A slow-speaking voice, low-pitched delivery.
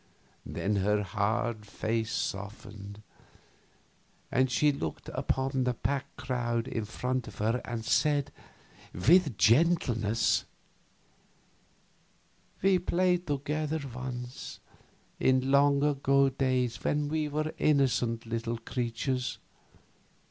Yes: slow, 100 wpm; low, 125 Hz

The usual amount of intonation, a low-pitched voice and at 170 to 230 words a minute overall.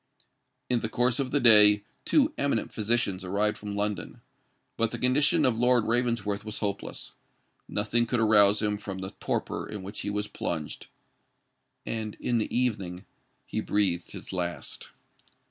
No: average, 3.0 semitones; low, 105 Hz; average, 155 wpm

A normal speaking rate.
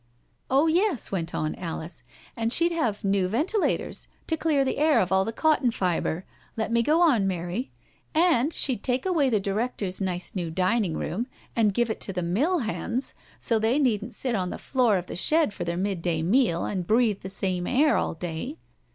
No: fast, 210 wpm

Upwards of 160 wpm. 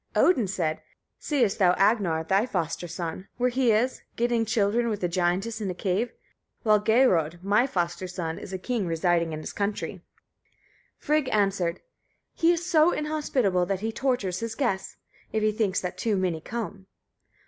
Yes: average, 170 wpm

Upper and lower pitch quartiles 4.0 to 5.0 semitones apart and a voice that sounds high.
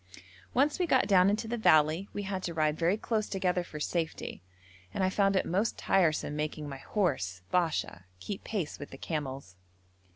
No: average, 4.7 semitones; medium, 180 Hz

